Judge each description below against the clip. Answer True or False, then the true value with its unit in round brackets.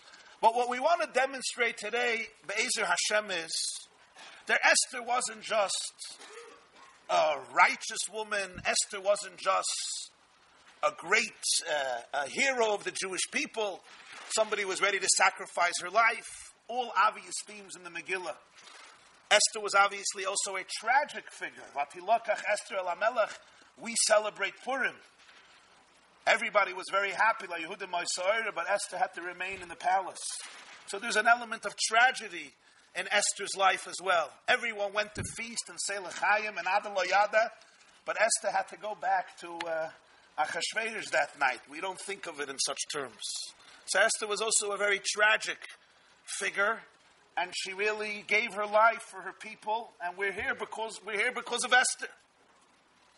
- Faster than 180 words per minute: False (145 wpm)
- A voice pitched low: False (205 Hz)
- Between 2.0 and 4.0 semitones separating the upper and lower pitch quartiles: True (3.2 semitones)